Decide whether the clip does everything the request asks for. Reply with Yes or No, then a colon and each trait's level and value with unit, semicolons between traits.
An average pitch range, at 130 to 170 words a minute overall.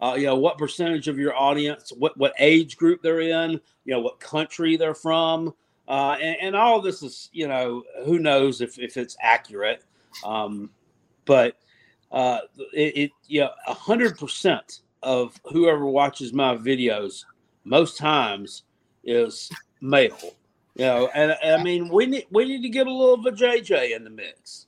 No: average, 4.0 semitones; average, 180 wpm